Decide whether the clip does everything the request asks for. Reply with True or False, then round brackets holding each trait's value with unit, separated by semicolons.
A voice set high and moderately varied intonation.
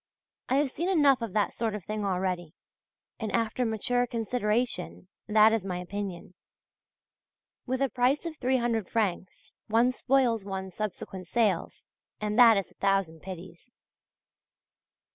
True (215 Hz; 4.3 semitones)